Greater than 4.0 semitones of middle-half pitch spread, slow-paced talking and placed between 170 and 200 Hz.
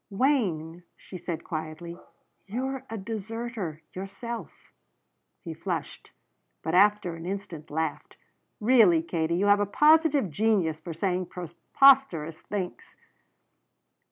Yes: average, 5.3 semitones; slow, 110 wpm; high, 190 Hz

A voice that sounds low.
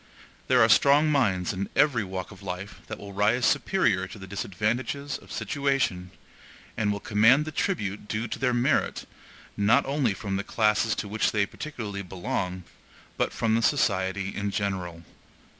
Yes: low, 105 Hz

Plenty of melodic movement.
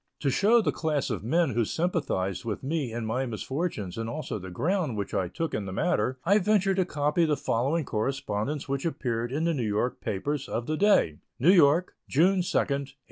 Yes: wide, 6.7 semitones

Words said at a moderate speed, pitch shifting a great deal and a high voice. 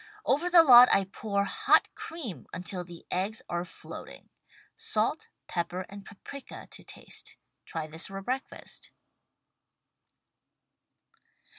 No: slow, 115 wpm; wide, 5.9 semitones; high, 195 Hz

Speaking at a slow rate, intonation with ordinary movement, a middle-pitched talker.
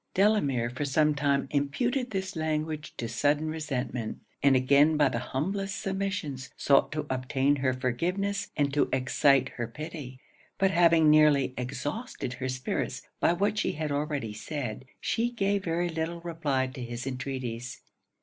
No: average, 150 wpm; average, 4.4 semitones; medium, 145 Hz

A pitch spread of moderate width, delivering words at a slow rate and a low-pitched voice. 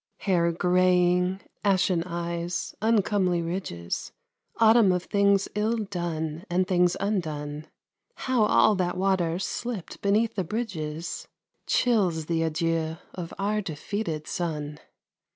No: average, 3.3 semitones; slow, 115 wpm; medium, 180 Hz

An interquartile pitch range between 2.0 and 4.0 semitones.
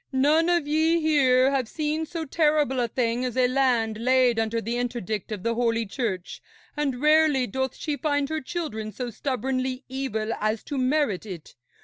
No: average, 4.5 semitones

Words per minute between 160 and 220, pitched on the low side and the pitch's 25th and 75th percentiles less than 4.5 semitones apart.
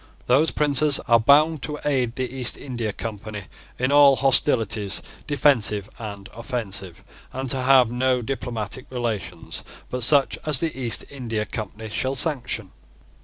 No: average, 140 wpm; low, 125 Hz; average, 3.8 semitones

